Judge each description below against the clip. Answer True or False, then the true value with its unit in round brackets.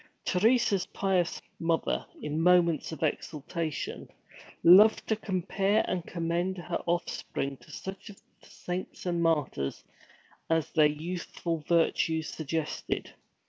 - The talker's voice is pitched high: False (170 Hz)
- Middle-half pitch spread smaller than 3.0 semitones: True (2.5 semitones)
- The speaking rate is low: True (115 wpm)